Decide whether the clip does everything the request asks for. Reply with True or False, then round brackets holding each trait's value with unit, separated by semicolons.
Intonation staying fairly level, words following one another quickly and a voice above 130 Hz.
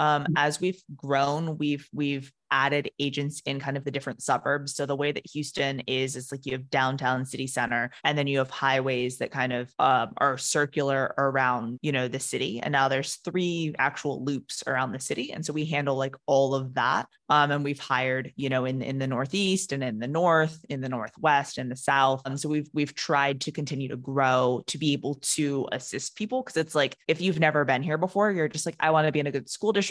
True (2.1 semitones; 235 wpm; 140 Hz)